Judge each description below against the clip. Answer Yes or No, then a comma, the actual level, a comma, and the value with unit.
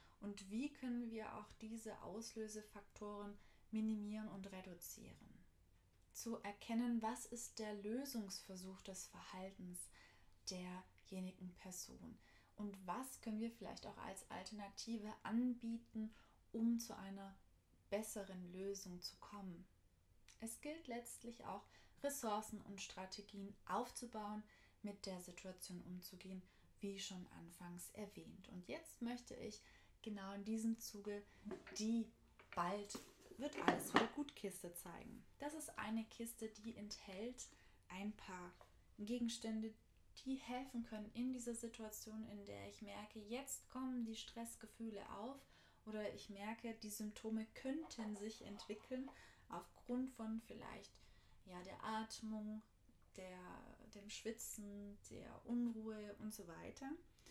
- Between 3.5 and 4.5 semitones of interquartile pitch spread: No, average, 2.8 semitones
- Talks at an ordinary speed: No, slow, 120 wpm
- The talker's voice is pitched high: Yes, high, 215 Hz